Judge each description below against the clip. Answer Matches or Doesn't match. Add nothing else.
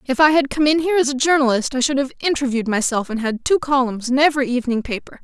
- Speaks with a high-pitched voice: Matches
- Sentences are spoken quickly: Matches